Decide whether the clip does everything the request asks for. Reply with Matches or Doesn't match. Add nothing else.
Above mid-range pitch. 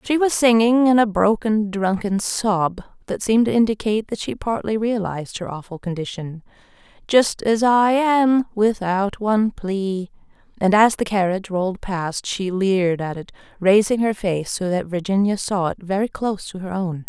Matches